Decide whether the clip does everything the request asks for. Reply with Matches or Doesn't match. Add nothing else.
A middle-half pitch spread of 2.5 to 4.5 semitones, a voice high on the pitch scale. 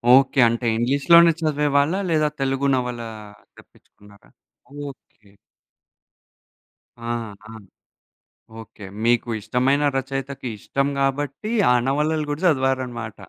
Doesn't match